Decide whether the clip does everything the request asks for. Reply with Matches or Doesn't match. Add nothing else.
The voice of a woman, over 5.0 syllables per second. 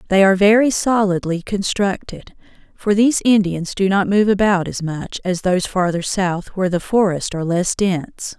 Matches